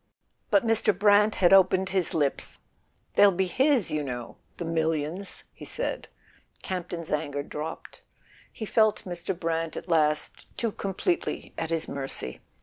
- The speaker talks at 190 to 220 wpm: No, average, 145 wpm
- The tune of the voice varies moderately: Yes, average, 4.1 semitones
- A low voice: No, medium, 175 Hz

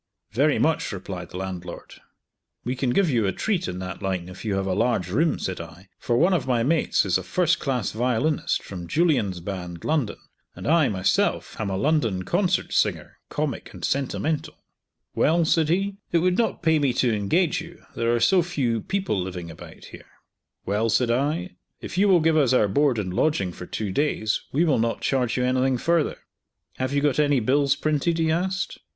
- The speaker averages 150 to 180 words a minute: No, average, 200 wpm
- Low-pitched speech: Yes, low, 130 Hz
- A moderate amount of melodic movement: No, wide, 8.4 semitones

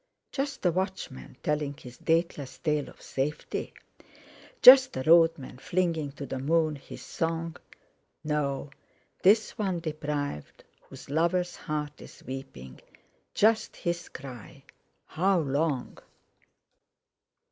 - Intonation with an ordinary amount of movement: Yes, average, 3.7 semitones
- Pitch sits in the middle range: Yes, medium, 155 Hz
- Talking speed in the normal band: No, slow, 115 wpm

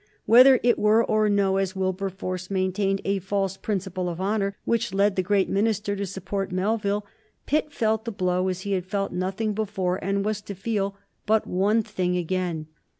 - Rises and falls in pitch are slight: Yes, narrow, 2.0 semitones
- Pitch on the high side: Yes, high, 195 Hz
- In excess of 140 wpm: Yes, average, 180 wpm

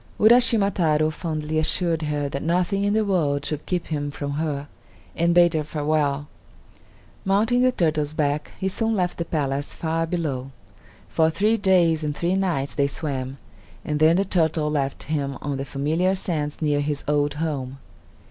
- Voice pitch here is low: No, medium, 155 Hz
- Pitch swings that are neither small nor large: Yes, average, 3.5 semitones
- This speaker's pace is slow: No, average, 170 wpm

